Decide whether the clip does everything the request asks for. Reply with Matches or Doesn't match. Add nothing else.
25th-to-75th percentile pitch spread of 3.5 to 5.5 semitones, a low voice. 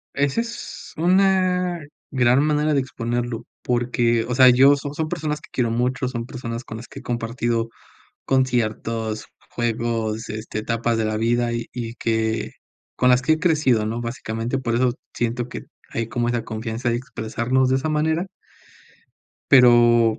Doesn't match